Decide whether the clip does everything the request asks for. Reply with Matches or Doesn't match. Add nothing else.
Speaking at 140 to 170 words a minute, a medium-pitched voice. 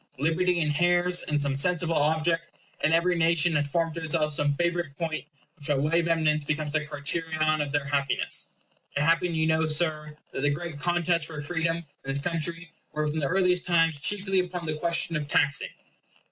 Doesn't match